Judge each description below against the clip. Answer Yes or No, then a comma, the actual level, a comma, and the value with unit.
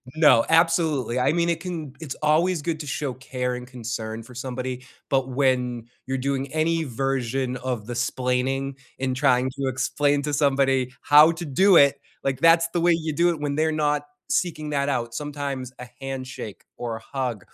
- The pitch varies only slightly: No, average, 3.3 semitones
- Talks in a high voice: No, low, 135 Hz